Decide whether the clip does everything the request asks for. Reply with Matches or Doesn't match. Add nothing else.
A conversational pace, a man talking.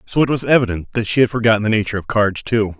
Doesn't match